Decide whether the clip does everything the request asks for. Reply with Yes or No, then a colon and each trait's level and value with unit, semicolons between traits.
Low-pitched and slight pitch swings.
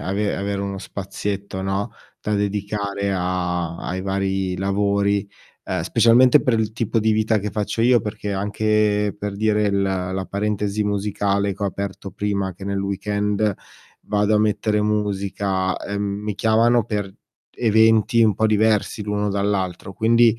Yes: low, 100 Hz; narrow, 1.4 semitones